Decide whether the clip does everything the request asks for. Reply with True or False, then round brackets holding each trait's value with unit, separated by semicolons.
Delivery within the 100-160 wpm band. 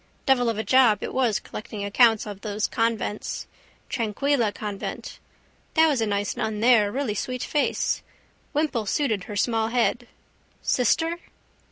True (145 wpm)